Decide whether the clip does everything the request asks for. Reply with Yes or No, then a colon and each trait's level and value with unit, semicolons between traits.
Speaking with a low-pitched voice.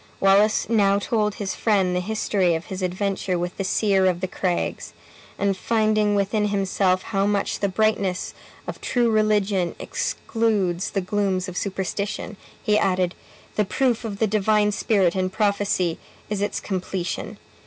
No: high, 200 Hz